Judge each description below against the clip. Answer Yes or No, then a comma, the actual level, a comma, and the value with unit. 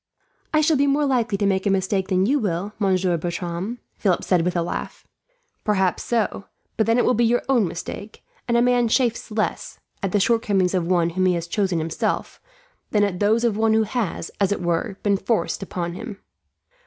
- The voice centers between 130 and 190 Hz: No, high, 200 Hz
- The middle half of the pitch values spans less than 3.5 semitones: No, average, 4.0 semitones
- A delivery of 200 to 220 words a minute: Yes, fast, 205 wpm